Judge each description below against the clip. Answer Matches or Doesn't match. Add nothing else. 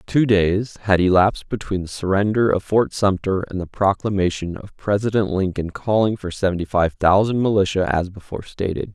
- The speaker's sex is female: Doesn't match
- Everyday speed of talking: Matches